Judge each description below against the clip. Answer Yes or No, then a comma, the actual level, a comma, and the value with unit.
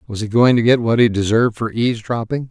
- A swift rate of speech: Yes, fast, 240 wpm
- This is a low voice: Yes, low, 115 Hz